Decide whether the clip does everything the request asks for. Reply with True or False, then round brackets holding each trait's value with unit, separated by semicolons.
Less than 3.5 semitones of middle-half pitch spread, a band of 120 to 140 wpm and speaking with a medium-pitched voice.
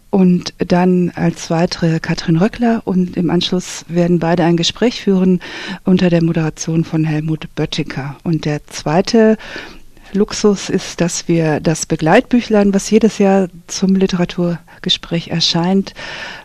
True (2.8 semitones; 130 wpm; 180 Hz)